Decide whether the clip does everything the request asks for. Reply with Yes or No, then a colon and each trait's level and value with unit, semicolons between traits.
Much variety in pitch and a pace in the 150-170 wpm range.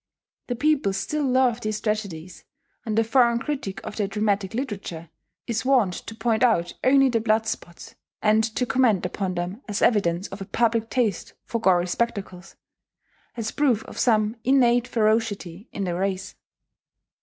No: average, 3.5 semitones; average, 160 wpm